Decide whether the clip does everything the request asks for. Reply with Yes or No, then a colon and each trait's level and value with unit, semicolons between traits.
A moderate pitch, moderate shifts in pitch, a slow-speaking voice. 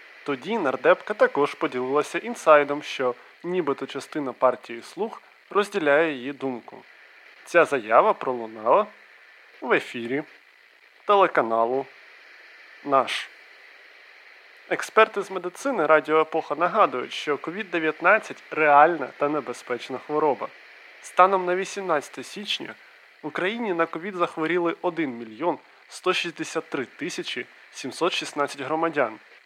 Yes: medium, 155 Hz; average, 4.1 semitones; slow, 95 wpm